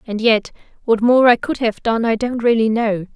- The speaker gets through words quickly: Yes, fast, 230 wpm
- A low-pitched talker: No, high, 230 Hz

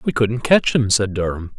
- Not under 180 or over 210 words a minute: No, fast, 230 wpm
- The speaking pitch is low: Yes, low, 110 Hz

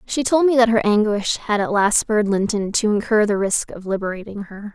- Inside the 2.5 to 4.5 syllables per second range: No, 5.4 syllables/s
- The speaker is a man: No, female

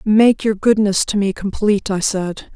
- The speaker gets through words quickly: No, average, 190 wpm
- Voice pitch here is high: Yes, high, 205 Hz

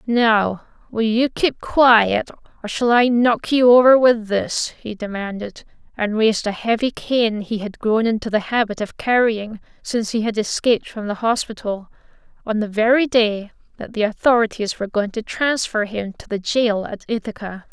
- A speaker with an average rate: Yes, average, 175 wpm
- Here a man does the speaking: No, female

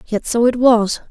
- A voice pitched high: Yes, high, 235 Hz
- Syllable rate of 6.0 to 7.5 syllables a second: No, 4.4 syllables/s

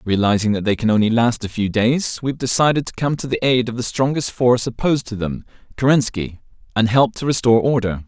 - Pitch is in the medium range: No, low, 120 Hz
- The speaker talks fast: Yes, fast, 210 wpm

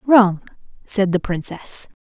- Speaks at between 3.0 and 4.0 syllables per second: Yes, 3.6 syllables/s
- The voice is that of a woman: Yes, female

